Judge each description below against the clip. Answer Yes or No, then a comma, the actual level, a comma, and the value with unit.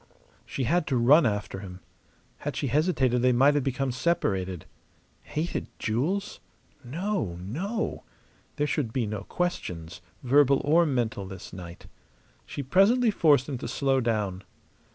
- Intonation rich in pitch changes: Yes, wide, 6.7 semitones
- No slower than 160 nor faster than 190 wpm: No, average, 140 wpm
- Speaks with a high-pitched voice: No, low, 130 Hz